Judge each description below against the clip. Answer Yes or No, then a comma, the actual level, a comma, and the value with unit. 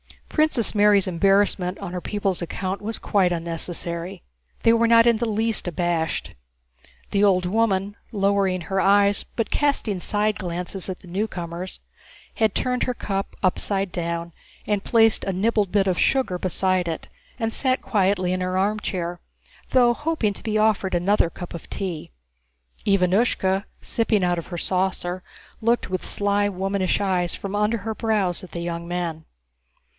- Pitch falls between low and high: No, high, 195 Hz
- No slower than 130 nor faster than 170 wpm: Yes, average, 160 wpm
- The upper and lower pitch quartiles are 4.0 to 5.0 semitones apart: No, average, 3.0 semitones